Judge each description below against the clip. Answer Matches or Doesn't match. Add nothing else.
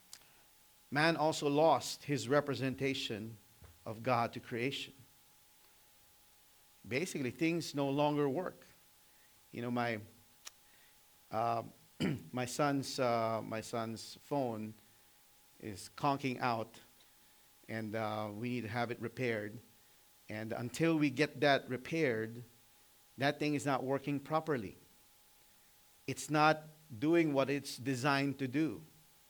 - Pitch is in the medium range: Doesn't match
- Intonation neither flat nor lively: Matches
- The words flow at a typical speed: Doesn't match